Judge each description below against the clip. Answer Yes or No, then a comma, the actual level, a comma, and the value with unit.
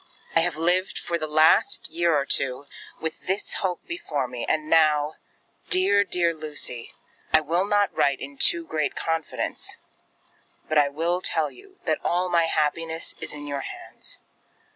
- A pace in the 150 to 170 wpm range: Yes, average, 165 wpm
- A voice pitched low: No, medium, 160 Hz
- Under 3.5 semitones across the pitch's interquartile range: Yes, average, 2.9 semitones